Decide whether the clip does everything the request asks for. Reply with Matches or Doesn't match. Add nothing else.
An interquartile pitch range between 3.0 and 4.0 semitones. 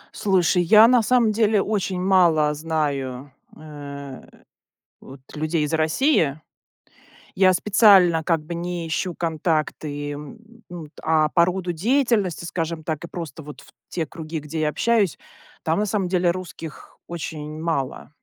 Matches